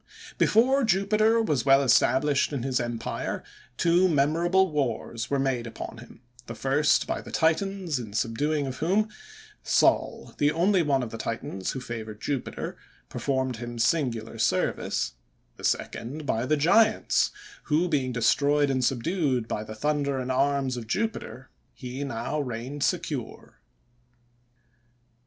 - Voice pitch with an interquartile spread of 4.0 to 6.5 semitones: Yes, average, 4.9 semitones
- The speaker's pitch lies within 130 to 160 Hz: Yes, low, 135 Hz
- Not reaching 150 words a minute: Yes, average, 140 wpm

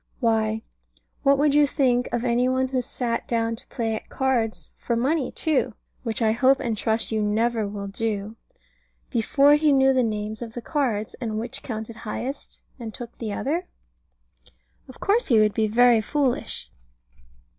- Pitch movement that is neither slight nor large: Yes, average, 3.2 semitones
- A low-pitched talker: No, high, 235 Hz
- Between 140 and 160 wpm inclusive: No, average, 170 wpm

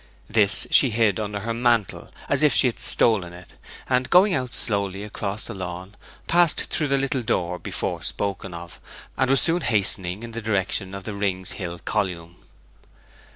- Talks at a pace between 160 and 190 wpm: Yes, average, 175 wpm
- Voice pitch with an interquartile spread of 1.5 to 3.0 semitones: No, average, 4.2 semitones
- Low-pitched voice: Yes, low, 105 Hz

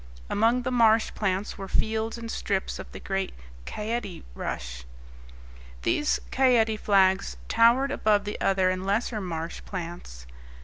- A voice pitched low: No, high, 205 Hz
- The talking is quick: No, slow, 135 wpm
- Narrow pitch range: No, average, 3.3 semitones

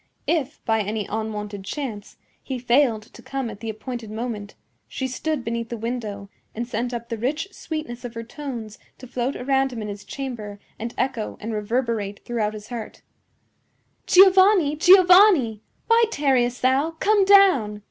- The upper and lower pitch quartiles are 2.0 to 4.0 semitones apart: No, average, 4.5 semitones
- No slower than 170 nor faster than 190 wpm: No, average, 160 wpm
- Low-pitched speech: No, high, 240 Hz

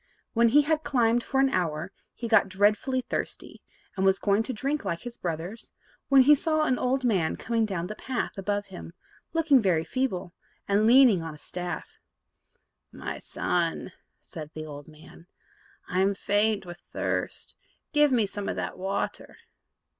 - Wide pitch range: Yes, wide, 6.3 semitones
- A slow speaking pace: No, average, 170 wpm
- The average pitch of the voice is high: Yes, high, 205 Hz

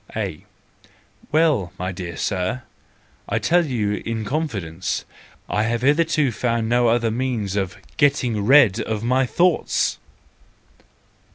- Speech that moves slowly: Yes, slow, 125 wpm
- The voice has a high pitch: No, low, 115 Hz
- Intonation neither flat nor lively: Yes, average, 4.6 semitones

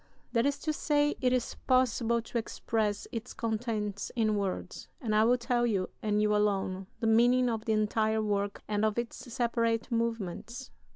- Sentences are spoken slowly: No, average, 175 wpm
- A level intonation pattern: Yes, narrow, 2.3 semitones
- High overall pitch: Yes, high, 225 Hz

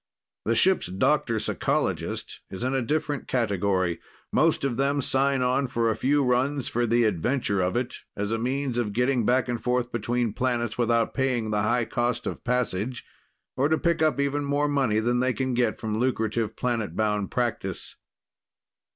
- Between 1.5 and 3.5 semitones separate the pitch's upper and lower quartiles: Yes, average, 3.1 semitones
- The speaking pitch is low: Yes, low, 120 Hz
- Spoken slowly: No, average, 175 wpm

